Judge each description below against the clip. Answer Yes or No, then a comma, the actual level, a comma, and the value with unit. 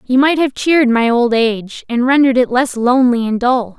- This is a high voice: Yes, very high, 250 Hz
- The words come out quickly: Yes, fast, 220 wpm